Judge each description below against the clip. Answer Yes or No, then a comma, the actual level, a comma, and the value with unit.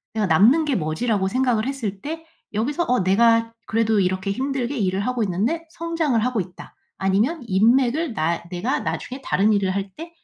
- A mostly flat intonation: No, wide, 5.6 semitones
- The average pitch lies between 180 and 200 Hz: No, high, 230 Hz